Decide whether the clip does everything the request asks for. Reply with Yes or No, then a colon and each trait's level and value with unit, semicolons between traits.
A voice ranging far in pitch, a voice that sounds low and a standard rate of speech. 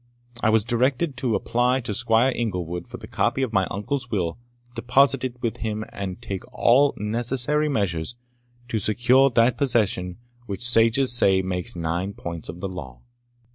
No: average, 4.6 semitones; low, 115 Hz; average, 160 wpm